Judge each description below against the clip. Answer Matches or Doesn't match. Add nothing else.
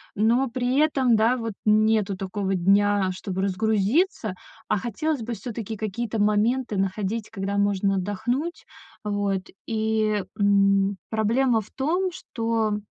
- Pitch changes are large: Doesn't match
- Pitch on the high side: Matches